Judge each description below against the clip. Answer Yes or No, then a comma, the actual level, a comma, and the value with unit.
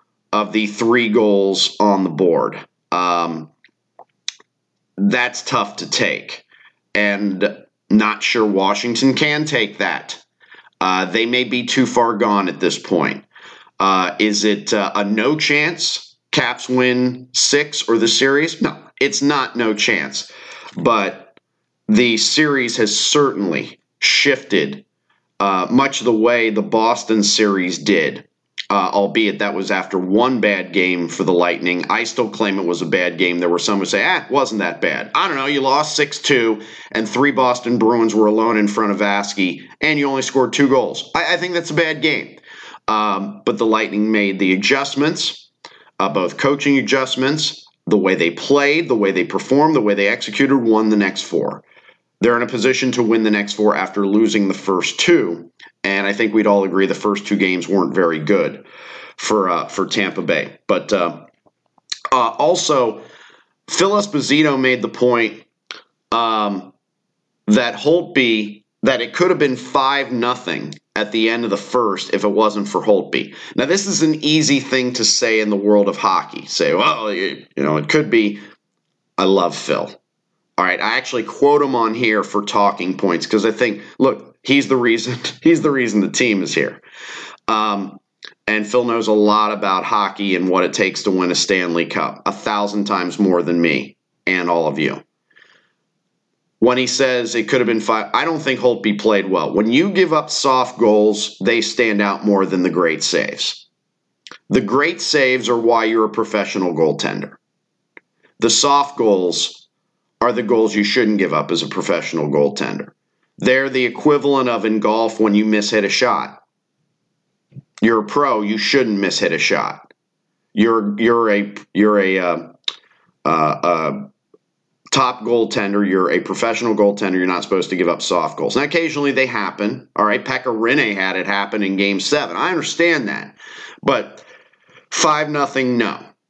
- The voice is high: No, low, 110 Hz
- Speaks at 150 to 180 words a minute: Yes, average, 175 wpm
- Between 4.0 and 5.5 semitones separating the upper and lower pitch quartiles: Yes, average, 4.3 semitones